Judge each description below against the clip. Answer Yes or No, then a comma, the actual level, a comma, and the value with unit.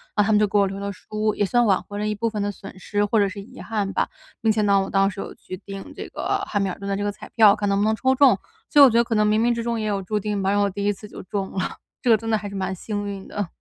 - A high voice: Yes, high, 205 Hz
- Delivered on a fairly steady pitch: Yes, narrow, 1.6 semitones